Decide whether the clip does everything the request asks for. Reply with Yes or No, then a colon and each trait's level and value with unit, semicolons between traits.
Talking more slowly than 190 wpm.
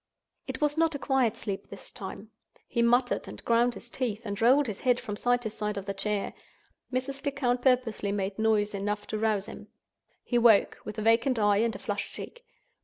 No: fast, 205 wpm